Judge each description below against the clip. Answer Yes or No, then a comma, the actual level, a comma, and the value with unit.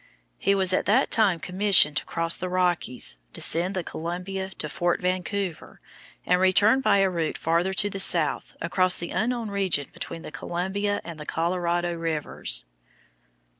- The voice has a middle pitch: Yes, medium, 180 Hz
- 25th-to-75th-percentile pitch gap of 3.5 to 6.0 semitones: No, narrow, 2.6 semitones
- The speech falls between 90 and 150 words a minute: No, average, 160 wpm